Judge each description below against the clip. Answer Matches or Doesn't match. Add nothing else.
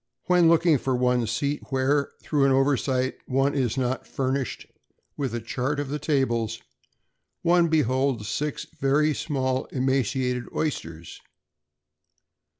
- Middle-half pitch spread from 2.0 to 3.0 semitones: Matches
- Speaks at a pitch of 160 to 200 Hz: Doesn't match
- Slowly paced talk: Matches